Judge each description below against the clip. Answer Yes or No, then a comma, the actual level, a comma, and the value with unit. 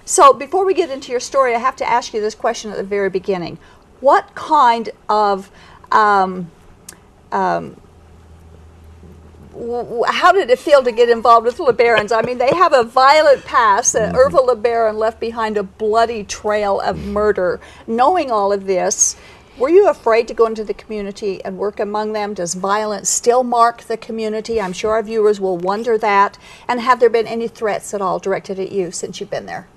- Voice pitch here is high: Yes, high, 220 Hz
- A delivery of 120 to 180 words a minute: No, average, 190 wpm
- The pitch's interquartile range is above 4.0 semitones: No, average, 3.4 semitones